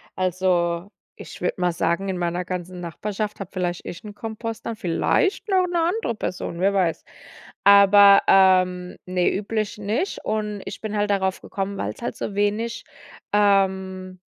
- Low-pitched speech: No, high, 195 Hz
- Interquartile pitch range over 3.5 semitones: No, narrow, 2.5 semitones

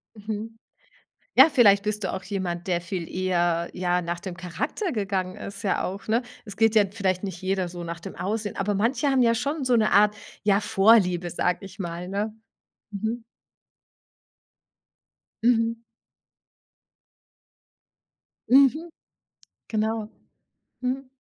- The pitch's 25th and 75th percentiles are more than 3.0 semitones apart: Yes, average, 3.7 semitones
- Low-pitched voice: No, high, 200 Hz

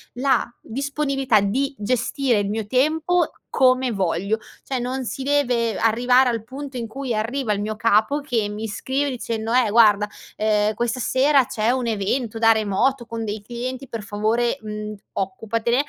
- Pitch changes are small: No, average, 3.5 semitones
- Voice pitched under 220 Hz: No, high, 235 Hz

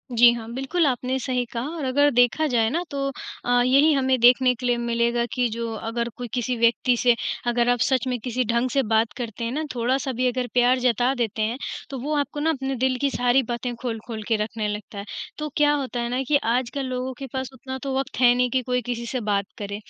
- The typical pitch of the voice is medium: No, high, 245 Hz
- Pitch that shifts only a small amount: Yes, narrow, 1.9 semitones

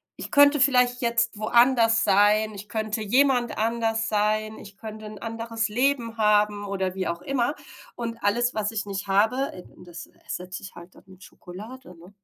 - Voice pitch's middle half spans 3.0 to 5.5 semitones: No, narrow, 2.6 semitones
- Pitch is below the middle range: No, high, 215 Hz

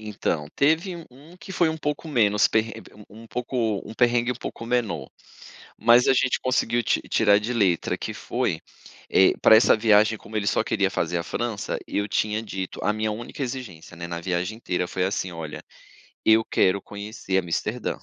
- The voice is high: No, low, 110 Hz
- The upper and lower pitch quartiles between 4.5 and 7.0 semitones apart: No, average, 4.0 semitones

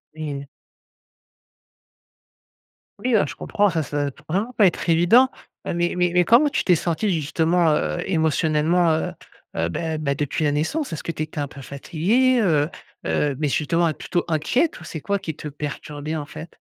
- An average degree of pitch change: Yes, average, 3.1 semitones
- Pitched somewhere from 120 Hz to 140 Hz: No, medium, 160 Hz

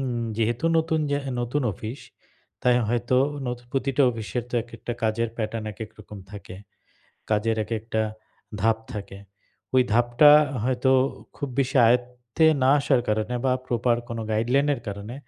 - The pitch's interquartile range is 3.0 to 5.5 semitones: No, narrow, 2.5 semitones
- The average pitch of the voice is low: Yes, low, 120 Hz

